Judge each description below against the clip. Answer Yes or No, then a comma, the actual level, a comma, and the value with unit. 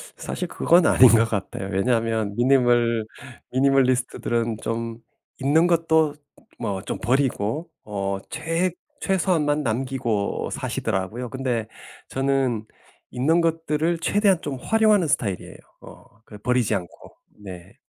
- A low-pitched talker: Yes, low, 130 Hz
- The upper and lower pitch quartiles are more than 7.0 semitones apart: No, wide, 6.1 semitones